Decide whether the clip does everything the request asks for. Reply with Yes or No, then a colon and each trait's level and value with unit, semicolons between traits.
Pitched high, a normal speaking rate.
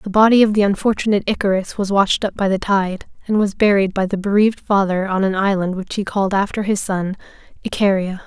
No: high, 200 Hz; fast, 210 wpm